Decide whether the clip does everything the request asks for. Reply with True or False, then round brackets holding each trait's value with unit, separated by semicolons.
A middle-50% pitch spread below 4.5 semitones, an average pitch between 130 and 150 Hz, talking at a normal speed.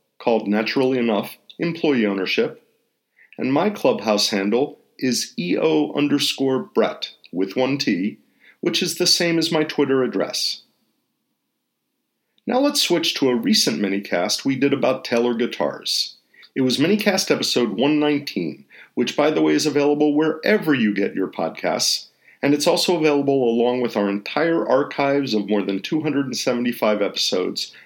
False (5.1 semitones; 140 Hz; 155 wpm)